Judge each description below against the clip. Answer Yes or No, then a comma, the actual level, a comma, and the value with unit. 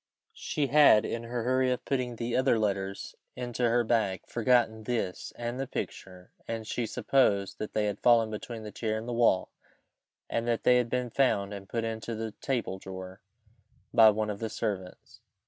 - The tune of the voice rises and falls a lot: No, average, 2.7 semitones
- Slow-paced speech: No, average, 185 wpm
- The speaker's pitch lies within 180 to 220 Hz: No, low, 115 Hz